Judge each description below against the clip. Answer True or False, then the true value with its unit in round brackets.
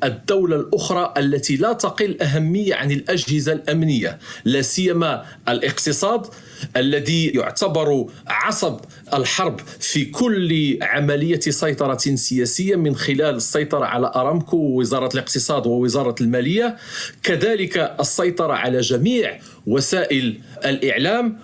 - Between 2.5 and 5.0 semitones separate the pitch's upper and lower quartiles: True (4.5 semitones)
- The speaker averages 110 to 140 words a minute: False (100 wpm)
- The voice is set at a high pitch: False (150 Hz)